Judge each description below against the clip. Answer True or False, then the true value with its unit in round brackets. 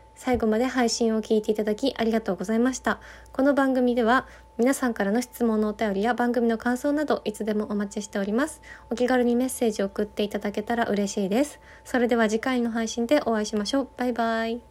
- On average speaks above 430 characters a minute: True (450 characters per minute)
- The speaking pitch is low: False (230 Hz)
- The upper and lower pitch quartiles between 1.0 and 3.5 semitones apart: True (2.4 semitones)